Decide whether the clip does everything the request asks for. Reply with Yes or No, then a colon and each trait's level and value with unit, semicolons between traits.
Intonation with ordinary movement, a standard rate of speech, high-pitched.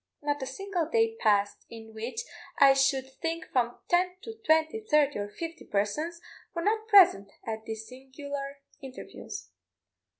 No: wide, 6.3 semitones; average, 145 wpm; very high, 280 Hz